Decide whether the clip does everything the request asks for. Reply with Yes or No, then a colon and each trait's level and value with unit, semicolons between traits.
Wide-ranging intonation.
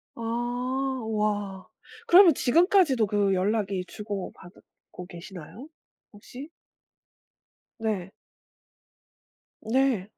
No: average, 4.7 semitones